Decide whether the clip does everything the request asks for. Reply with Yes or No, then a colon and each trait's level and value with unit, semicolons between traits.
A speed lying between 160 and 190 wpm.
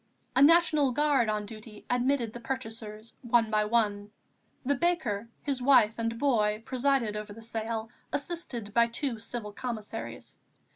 No: average, 145 wpm